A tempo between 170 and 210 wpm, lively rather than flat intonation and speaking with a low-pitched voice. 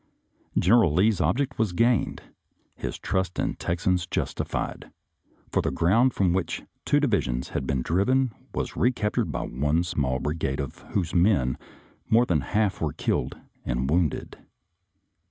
No: average, 155 wpm; wide, 6.9 semitones; very low, 90 Hz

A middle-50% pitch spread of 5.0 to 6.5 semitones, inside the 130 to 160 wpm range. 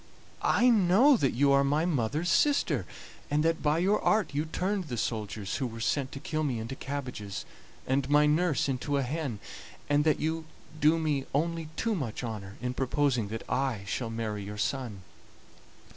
No: wide, 5.4 semitones; average, 180 wpm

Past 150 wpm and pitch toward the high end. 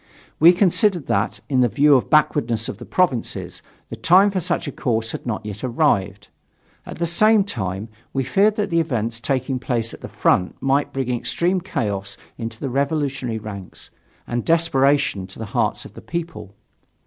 No: average, 180 wpm; low, 135 Hz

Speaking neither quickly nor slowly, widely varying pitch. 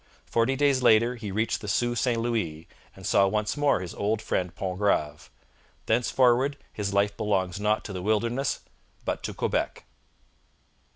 No: average, 155 wpm; average, 3.5 semitones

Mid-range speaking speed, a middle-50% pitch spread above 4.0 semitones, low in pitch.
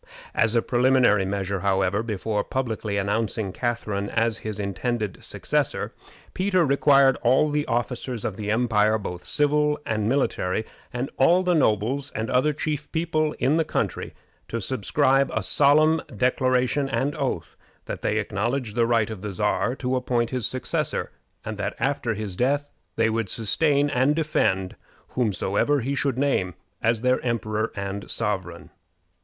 Yes: average, 150 wpm; average, 4.7 semitones; low, 120 Hz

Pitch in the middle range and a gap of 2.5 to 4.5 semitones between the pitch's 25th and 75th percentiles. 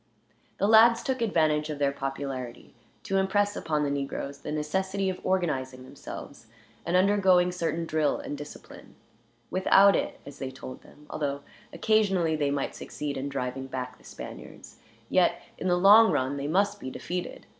No: medium, 155 Hz; wide, 5.4 semitones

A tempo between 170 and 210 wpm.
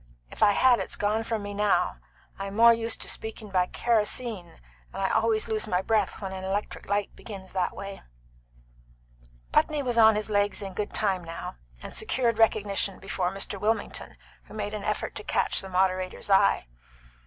Yes: average, 180 wpm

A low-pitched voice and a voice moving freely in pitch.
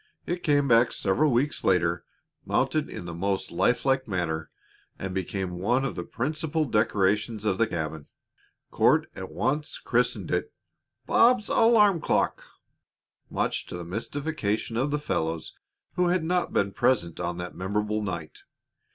Yes: low, 110 Hz; wide, 8.2 semitones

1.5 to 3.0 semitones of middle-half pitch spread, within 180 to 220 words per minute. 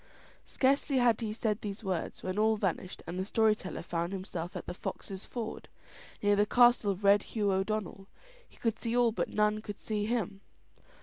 Yes: narrow, 2.5 semitones; average, 190 wpm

